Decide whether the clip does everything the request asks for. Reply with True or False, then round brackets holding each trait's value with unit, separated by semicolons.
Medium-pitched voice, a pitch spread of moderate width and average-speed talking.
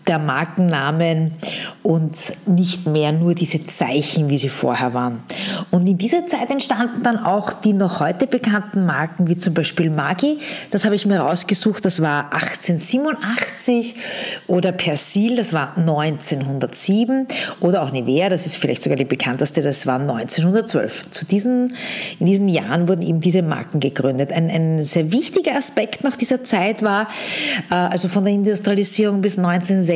True (180 Hz; 4.9 semitones; 155 wpm)